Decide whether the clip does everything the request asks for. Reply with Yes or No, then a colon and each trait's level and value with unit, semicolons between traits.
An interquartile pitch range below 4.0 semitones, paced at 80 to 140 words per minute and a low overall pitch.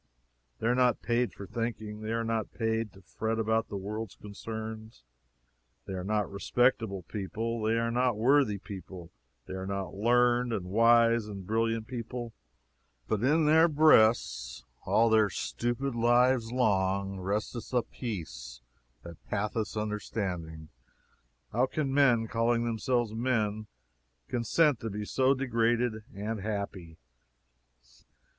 Yes: average, 2.9 semitones; slow, 135 wpm; low, 110 Hz